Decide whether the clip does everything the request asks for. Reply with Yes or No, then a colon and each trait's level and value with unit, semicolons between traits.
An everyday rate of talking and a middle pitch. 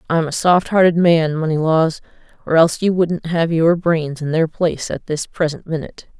Yes: average, 185 wpm; medium, 165 Hz